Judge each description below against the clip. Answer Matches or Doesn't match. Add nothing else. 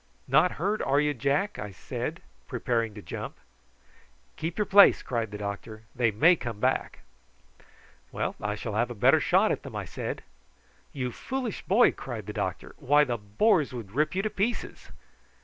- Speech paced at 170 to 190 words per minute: Matches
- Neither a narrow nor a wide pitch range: Doesn't match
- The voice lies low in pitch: Matches